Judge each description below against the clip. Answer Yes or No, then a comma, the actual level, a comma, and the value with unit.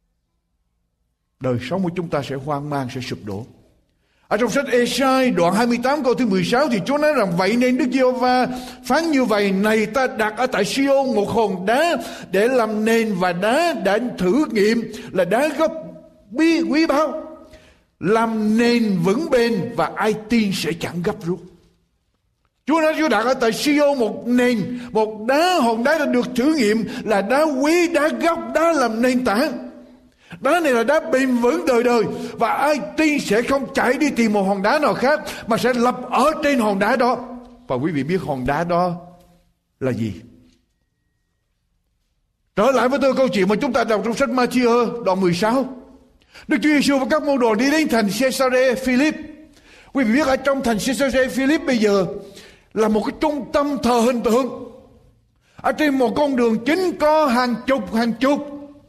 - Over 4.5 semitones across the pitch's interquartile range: Yes, average, 5.1 semitones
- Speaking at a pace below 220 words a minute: Yes, average, 190 wpm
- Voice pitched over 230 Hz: Yes, high, 245 Hz